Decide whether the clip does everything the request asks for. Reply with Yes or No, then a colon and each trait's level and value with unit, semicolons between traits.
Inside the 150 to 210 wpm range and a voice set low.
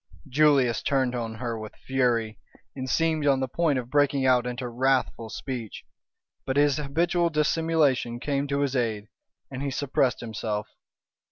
Yes: average, 155 wpm; low, 130 Hz